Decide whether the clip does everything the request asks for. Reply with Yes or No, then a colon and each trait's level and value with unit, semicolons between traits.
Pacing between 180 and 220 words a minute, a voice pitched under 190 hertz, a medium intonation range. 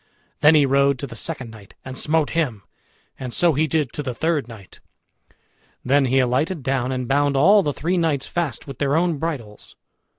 Yes: average, 195 wpm; medium, 140 Hz; average, 3.8 semitones